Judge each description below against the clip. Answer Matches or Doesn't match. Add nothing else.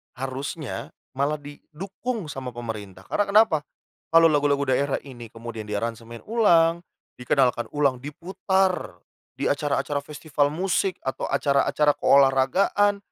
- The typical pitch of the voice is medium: Matches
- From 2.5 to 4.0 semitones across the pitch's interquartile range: Doesn't match